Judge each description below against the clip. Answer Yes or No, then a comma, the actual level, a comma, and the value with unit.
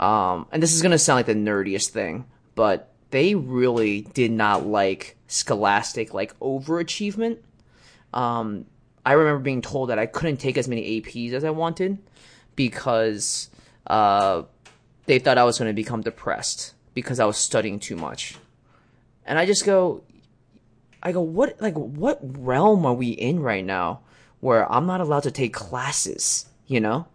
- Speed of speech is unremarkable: Yes, average, 165 wpm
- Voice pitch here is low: Yes, low, 125 Hz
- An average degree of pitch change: No, wide, 6.5 semitones